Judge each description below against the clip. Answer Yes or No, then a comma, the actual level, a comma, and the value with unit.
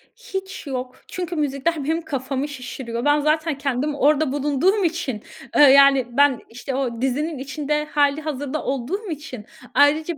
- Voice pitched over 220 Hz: Yes, very high, 290 Hz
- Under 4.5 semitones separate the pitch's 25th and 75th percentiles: Yes, average, 2.9 semitones